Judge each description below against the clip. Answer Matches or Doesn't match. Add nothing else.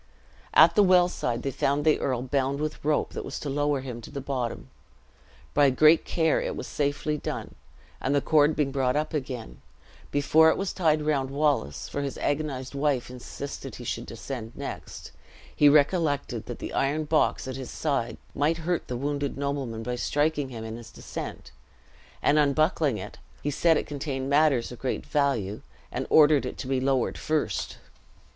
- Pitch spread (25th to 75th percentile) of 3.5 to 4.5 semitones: Doesn't match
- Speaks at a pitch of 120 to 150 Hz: Matches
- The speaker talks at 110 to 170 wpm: Doesn't match